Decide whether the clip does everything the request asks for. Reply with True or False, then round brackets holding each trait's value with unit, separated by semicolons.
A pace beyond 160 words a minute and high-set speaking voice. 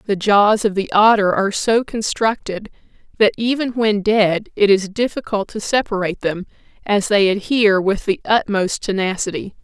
False (155 wpm; 205 Hz)